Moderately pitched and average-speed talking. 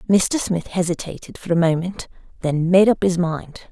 Yes: medium, 175 Hz; average, 180 wpm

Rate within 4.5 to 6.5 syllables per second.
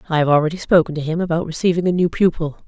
No: 7.4 syllables/s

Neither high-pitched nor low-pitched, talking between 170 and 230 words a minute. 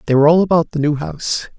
No: medium, 155 Hz; fast, 265 wpm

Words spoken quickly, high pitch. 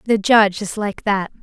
Yes: fast, 210 wpm; high, 205 Hz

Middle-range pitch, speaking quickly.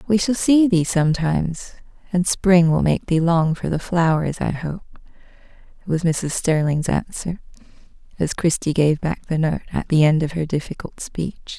No: medium, 170 Hz; average, 170 wpm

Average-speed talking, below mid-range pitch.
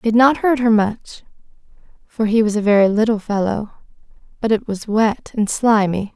No: average, 185 wpm; high, 215 Hz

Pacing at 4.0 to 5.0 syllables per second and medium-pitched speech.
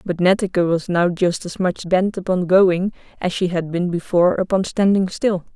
Yes: 4.9 syllables/s; medium, 180 Hz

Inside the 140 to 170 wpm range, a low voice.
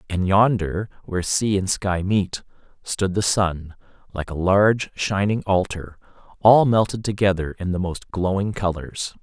Yes: average, 150 wpm; very low, 95 Hz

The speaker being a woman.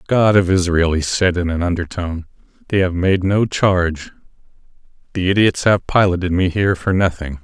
No: male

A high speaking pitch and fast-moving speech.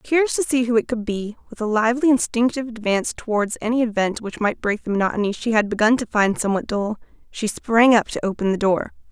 Yes: high, 225 Hz; fast, 225 wpm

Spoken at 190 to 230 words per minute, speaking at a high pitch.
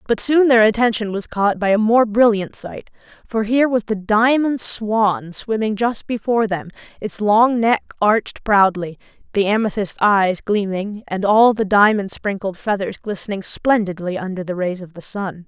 No: average, 170 wpm; high, 210 Hz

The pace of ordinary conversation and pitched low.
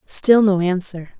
No: average, 150 wpm; high, 190 Hz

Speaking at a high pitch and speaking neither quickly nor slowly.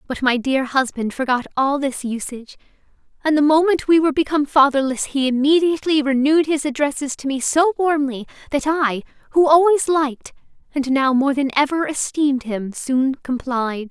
Yes: very high, 280 Hz; average, 165 wpm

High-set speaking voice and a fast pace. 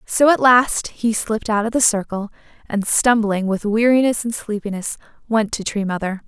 No: high, 220 Hz; average, 180 wpm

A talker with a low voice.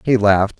Yes: low, 105 Hz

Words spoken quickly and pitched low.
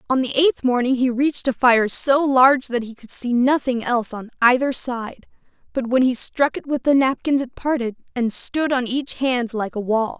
No: fast, 220 wpm; very high, 250 Hz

